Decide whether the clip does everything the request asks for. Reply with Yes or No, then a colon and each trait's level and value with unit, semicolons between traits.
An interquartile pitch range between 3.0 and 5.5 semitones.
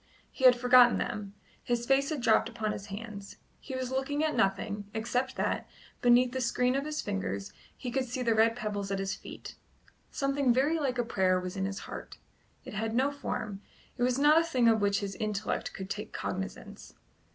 Yes: average, 4.3 semitones